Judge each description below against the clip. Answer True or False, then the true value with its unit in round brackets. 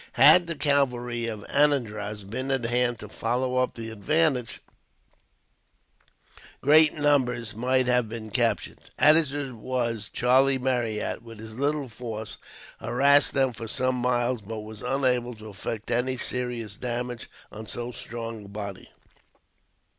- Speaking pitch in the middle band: False (120 Hz)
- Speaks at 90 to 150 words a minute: True (140 wpm)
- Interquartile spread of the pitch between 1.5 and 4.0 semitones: True (2.7 semitones)